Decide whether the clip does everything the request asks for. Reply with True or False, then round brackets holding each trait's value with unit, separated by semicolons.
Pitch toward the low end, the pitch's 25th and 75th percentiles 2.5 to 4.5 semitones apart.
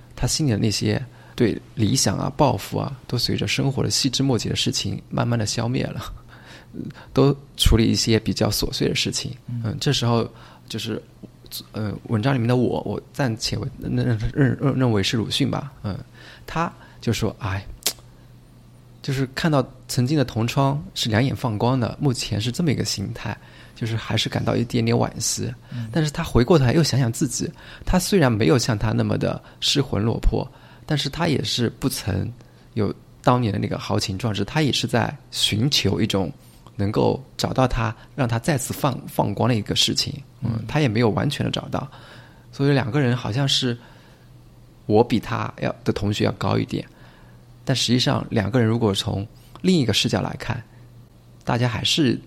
True (120 Hz; 3.4 semitones)